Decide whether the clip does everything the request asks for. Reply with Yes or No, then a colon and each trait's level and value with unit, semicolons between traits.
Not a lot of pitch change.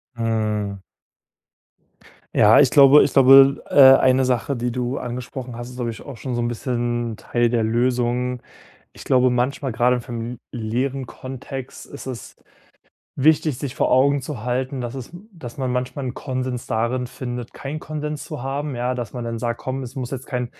Yes: narrow, 1.9 semitones